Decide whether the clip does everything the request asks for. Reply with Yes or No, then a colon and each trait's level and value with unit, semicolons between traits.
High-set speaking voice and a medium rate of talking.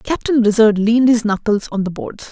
No: high, 225 Hz; fast, 210 wpm